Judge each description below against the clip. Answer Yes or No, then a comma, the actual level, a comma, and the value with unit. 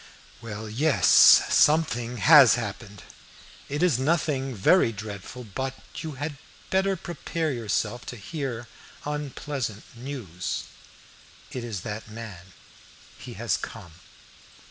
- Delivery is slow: Yes, slow, 110 wpm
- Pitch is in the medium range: No, low, 125 Hz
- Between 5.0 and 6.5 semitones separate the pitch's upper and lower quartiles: Yes, average, 5.3 semitones